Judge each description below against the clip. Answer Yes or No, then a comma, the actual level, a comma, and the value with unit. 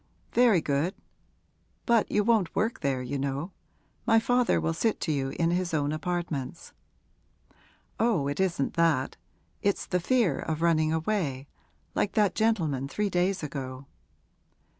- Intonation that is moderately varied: No, wide, 6.4 semitones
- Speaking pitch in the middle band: Yes, medium, 170 Hz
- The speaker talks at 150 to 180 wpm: No, average, 140 wpm